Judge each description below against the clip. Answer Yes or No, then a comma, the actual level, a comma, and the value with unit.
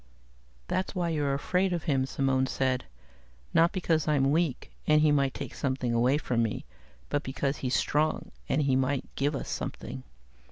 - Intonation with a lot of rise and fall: No, average, 2.9 semitones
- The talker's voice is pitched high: No, medium, 140 Hz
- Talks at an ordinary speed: Yes, average, 170 wpm